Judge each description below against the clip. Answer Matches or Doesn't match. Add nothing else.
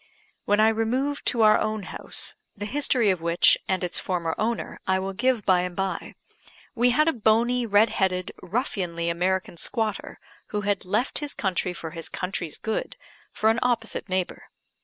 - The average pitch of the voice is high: Matches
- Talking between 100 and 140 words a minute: Doesn't match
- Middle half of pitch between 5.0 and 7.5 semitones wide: Doesn't match